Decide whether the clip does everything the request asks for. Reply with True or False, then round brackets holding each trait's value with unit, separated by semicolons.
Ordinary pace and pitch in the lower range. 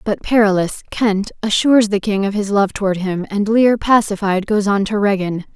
False (175 wpm; 205 Hz)